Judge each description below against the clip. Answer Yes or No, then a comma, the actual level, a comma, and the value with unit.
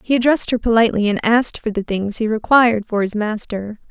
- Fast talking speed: Yes, fast, 215 wpm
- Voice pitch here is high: Yes, high, 220 Hz